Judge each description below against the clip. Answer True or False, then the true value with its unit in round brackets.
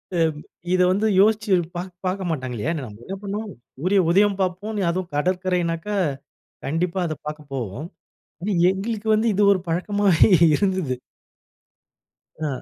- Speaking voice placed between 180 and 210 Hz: True (185 Hz)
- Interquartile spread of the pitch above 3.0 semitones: True (3.9 semitones)